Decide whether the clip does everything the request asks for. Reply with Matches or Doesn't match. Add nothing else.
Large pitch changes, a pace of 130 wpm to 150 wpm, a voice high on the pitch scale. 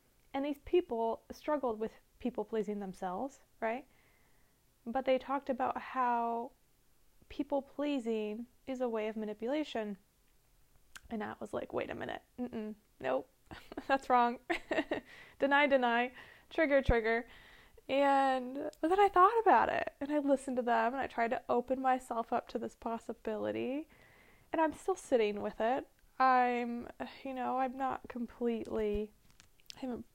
Doesn't match